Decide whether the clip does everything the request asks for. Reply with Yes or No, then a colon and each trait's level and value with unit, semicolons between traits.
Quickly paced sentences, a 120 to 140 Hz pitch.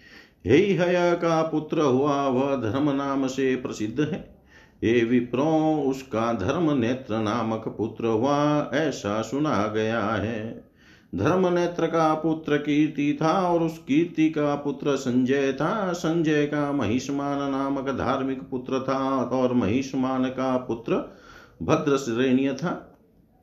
No: average, 125 wpm; low, 135 Hz